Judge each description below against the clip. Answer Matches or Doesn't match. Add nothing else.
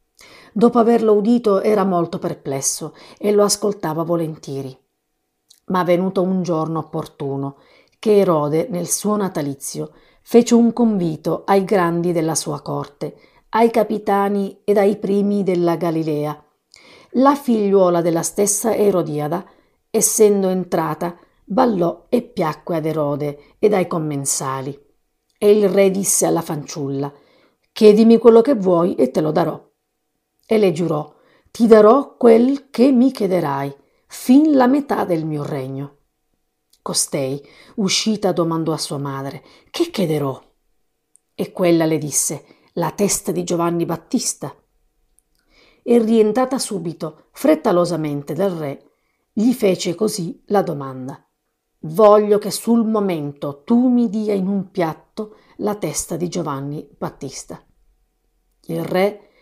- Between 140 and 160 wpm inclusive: Doesn't match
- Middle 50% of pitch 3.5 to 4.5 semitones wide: Doesn't match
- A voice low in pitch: Doesn't match